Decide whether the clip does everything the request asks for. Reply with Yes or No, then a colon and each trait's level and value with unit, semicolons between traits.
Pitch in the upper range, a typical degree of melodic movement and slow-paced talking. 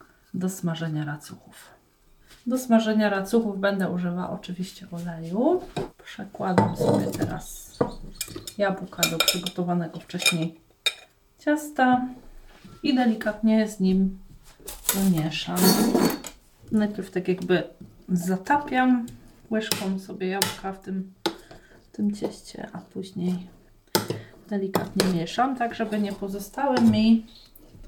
Yes: high, 195 Hz; average, 3.5 semitones; slow, 95 wpm